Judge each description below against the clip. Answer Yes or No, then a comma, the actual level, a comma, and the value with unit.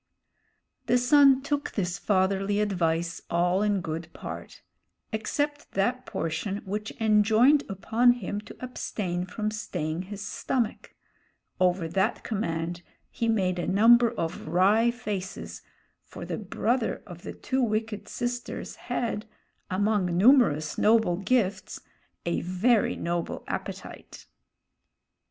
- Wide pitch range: No, average, 4.4 semitones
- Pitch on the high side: Yes, high, 205 Hz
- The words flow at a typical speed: No, slow, 120 wpm